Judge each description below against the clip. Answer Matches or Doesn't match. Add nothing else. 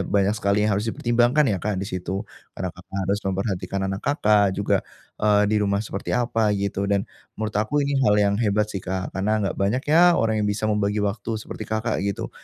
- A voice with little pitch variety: Matches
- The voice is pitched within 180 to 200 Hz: Doesn't match